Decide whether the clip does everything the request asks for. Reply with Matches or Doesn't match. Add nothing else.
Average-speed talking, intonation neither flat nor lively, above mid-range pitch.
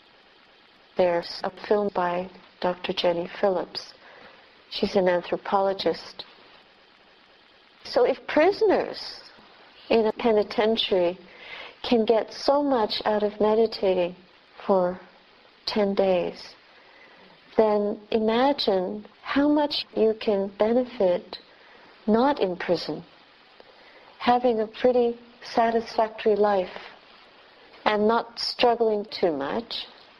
Doesn't match